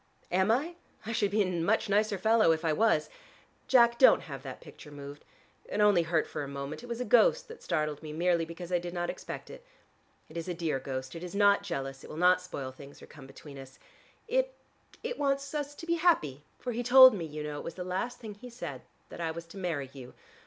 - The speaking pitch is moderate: Yes, medium, 180 Hz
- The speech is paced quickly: Yes, fast, 240 wpm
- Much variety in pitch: Yes, wide, 7.6 semitones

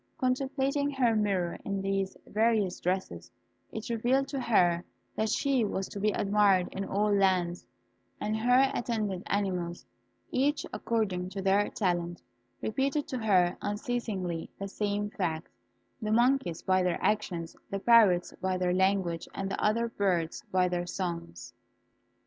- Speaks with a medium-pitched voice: No, high, 200 Hz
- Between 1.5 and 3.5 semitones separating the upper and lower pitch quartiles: No, average, 4.0 semitones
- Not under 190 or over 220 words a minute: No, average, 145 wpm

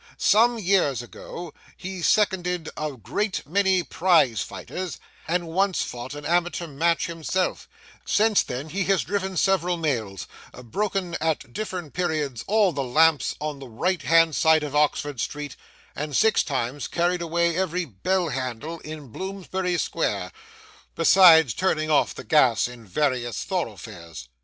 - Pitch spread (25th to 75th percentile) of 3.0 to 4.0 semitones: No, average, 4.6 semitones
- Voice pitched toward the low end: No, medium, 165 Hz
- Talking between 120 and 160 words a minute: Yes, average, 140 wpm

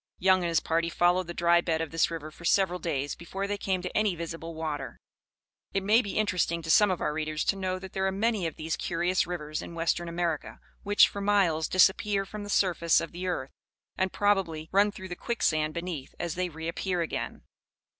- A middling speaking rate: No, fast, 215 wpm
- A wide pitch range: No, average, 2.7 semitones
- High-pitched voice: No, medium, 175 Hz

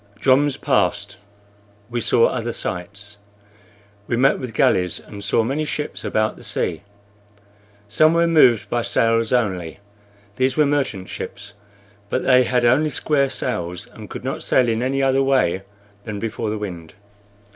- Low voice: Yes, low, 120 Hz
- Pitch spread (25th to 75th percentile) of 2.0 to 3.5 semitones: No, average, 4.7 semitones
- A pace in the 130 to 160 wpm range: Yes, average, 155 wpm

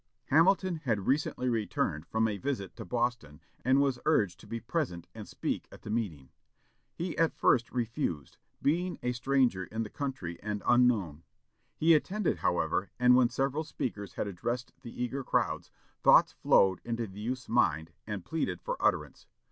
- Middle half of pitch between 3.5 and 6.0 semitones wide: Yes, average, 5.2 semitones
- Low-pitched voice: Yes, low, 120 Hz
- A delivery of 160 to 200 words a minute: Yes, average, 165 wpm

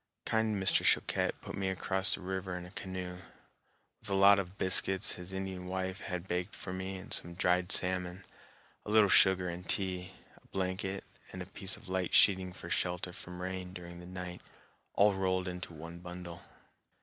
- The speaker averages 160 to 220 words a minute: Yes, average, 185 wpm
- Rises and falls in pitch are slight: Yes, narrow, 1.1 semitones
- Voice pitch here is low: Yes, very low, 95 Hz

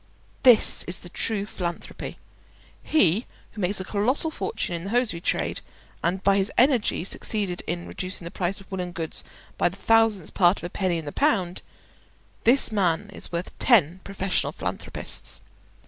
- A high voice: Yes, high, 195 Hz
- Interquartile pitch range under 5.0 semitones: Yes, average, 3.8 semitones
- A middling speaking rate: Yes, average, 165 wpm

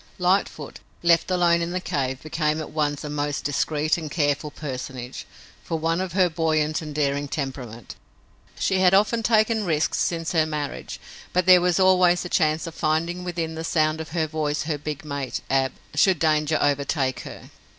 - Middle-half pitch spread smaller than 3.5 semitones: Yes, average, 3.1 semitones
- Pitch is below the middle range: No, medium, 155 Hz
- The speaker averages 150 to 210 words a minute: Yes, average, 180 wpm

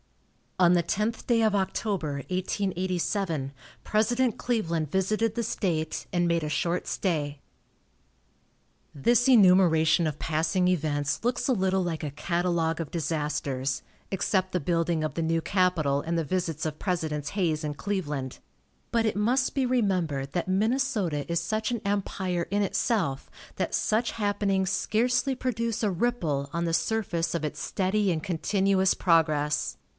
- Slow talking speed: No, average, 150 wpm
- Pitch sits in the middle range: Yes, medium, 180 Hz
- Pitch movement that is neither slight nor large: Yes, average, 4.7 semitones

